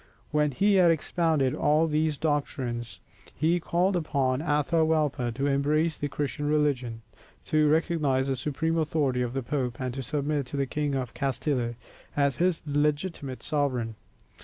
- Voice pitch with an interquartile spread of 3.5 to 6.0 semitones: No, average, 2.9 semitones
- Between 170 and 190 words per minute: No, average, 150 wpm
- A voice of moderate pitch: Yes, medium, 145 Hz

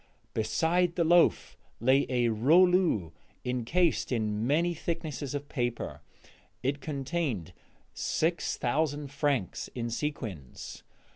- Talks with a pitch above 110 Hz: Yes, medium, 140 Hz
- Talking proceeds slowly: Yes, slow, 100 wpm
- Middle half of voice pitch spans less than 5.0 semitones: No, wide, 5.6 semitones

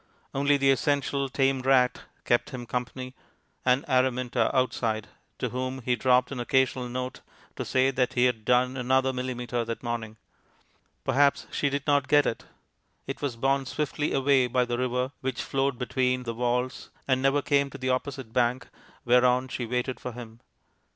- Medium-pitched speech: No, low, 130 Hz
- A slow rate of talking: No, average, 170 wpm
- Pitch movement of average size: No, narrow, 1.5 semitones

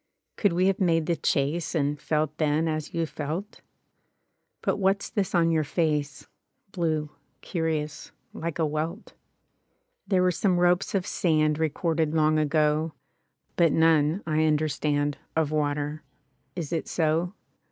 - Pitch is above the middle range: No, medium, 160 Hz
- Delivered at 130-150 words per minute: Yes, average, 145 wpm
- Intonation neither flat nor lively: No, narrow, 2.0 semitones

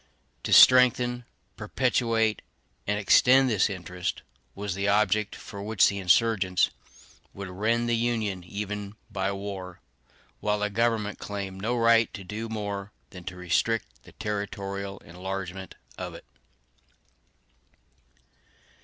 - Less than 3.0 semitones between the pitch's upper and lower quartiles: Yes, narrow, 2.5 semitones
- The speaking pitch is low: Yes, low, 105 Hz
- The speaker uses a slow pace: Yes, slow, 120 wpm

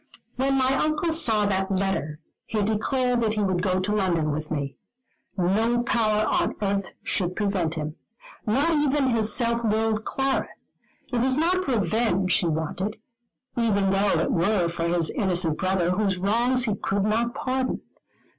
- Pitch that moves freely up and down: No, average, 4.5 semitones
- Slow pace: No, average, 160 wpm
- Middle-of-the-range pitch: No, high, 210 Hz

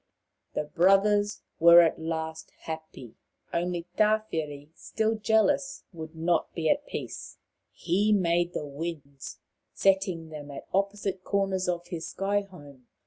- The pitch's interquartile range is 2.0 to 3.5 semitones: No, average, 3.9 semitones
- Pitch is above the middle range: No, medium, 175 Hz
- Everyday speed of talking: No, slow, 130 wpm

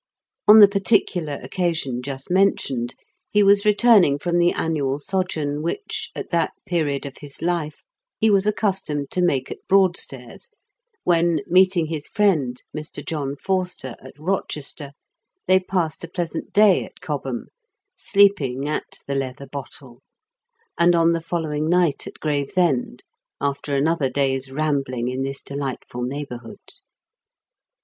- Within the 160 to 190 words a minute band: No, slow, 135 wpm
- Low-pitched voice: No, medium, 155 Hz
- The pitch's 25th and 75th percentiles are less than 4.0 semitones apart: No, average, 4.7 semitones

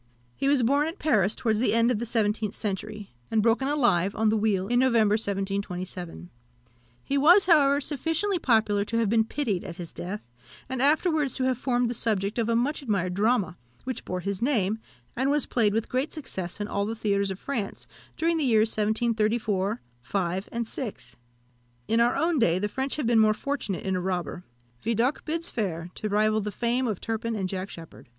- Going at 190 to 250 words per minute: Yes, average, 200 wpm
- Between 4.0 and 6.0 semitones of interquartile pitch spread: Yes, average, 4.4 semitones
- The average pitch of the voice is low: No, high, 220 Hz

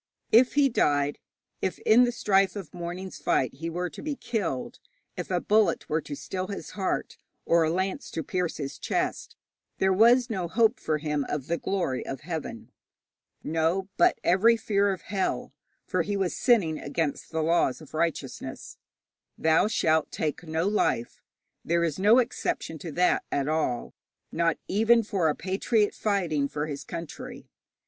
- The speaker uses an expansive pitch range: No, average, 4.4 semitones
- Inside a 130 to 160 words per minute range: No, average, 170 wpm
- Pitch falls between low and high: Yes, medium, 175 Hz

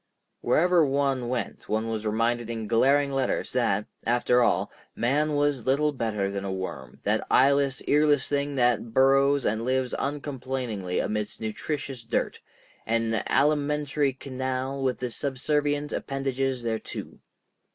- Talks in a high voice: No, low, 130 Hz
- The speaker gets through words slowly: Yes, slow, 130 wpm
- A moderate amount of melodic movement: Yes, average, 3.5 semitones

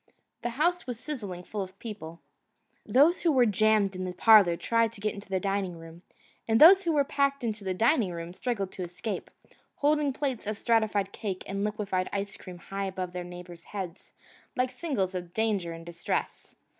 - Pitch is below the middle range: No, high, 205 Hz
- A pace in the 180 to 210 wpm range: Yes, average, 190 wpm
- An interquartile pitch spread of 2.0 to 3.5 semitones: No, average, 4.7 semitones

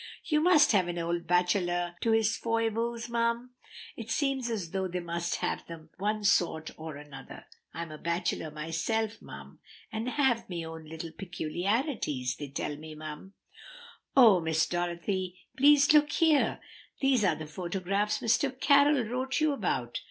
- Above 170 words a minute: No, average, 160 wpm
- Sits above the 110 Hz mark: Yes, high, 190 Hz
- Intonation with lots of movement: Yes, wide, 6.1 semitones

